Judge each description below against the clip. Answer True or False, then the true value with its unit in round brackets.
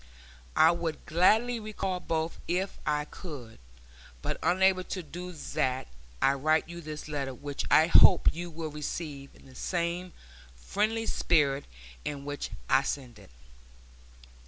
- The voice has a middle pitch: True (160 Hz)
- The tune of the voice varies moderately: True (3.9 semitones)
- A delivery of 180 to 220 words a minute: False (140 wpm)